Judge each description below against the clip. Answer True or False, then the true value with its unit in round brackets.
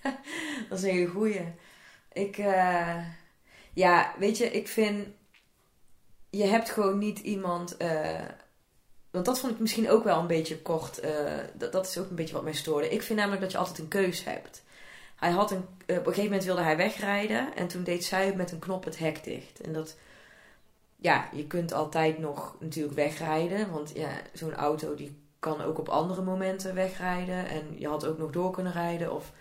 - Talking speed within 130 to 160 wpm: False (195 wpm)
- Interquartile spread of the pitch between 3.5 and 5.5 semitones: True (3.9 semitones)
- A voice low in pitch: False (180 Hz)